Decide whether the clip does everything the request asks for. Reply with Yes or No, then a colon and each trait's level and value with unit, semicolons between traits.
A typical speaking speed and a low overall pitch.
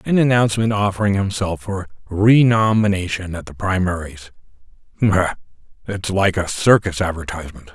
No: slow, 110 wpm; very low, 95 Hz